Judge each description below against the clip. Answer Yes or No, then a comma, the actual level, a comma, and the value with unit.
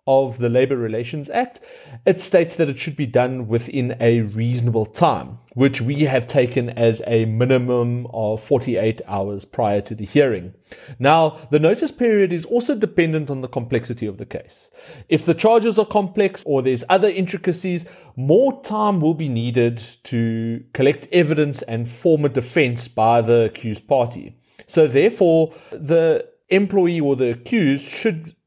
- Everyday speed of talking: Yes, average, 160 wpm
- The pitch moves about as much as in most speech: No, wide, 6.6 semitones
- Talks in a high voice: No, low, 135 Hz